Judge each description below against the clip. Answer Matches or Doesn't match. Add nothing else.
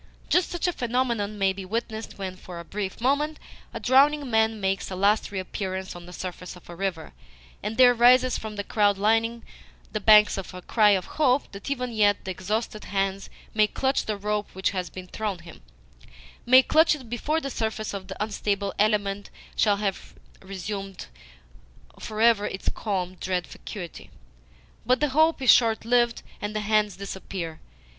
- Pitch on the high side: Matches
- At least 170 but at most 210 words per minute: Matches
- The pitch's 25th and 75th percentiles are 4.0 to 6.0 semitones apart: Doesn't match